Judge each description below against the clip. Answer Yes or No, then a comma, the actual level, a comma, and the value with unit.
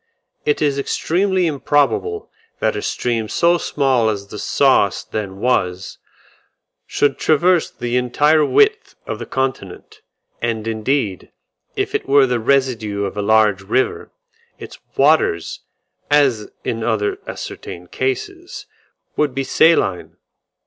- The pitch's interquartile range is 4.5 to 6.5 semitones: Yes, wide, 5.4 semitones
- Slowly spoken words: Yes, slow, 125 wpm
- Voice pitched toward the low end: Yes, low, 130 Hz